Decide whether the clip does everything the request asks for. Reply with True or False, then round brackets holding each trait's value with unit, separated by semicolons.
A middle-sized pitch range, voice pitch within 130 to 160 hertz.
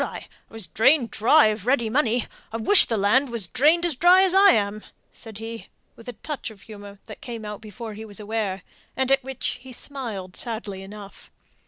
False (4.1 semitones; 225 Hz)